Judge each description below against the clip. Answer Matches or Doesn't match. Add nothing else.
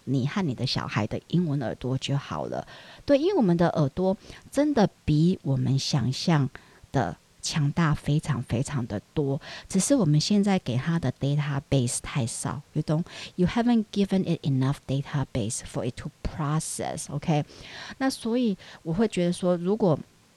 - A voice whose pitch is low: Doesn't match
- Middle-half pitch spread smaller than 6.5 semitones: Matches